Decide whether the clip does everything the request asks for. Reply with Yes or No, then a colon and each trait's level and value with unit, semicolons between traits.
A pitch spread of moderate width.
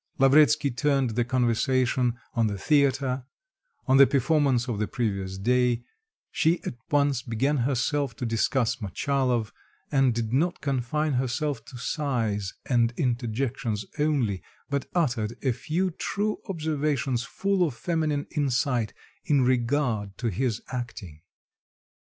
Yes: average, 3.5 semitones